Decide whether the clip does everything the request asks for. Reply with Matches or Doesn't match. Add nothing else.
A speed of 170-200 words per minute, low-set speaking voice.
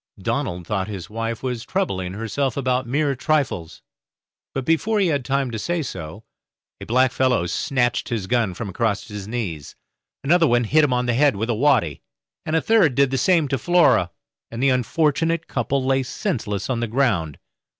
Matches